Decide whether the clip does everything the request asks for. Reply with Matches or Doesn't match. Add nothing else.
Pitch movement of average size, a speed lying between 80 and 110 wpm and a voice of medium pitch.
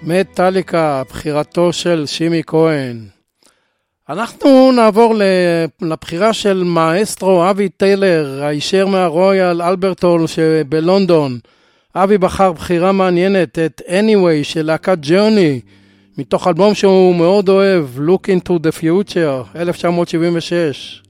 Matches